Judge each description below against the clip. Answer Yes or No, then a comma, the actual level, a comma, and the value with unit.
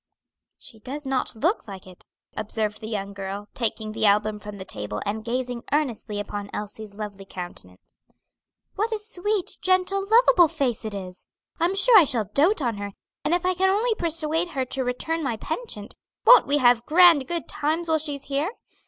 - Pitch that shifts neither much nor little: No, wide, 8.4 semitones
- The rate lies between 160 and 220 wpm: Yes, average, 185 wpm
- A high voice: Yes, very high, 260 Hz